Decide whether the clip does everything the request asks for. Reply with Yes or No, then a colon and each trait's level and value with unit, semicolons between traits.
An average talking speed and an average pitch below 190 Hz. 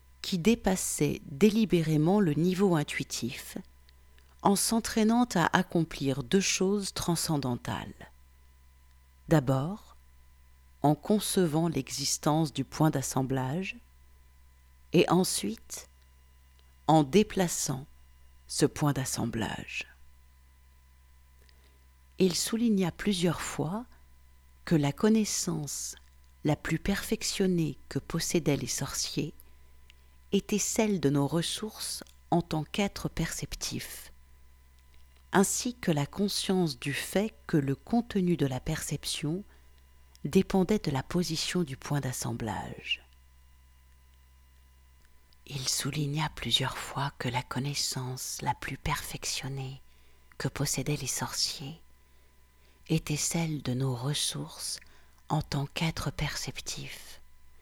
No: slow, 95 wpm; low, 135 Hz